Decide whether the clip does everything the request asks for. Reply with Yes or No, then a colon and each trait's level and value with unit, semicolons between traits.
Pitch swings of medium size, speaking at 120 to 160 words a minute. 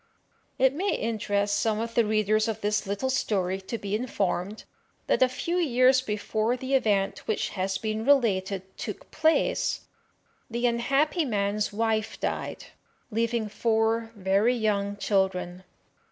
Yes: average, 3.2 semitones; average, 140 wpm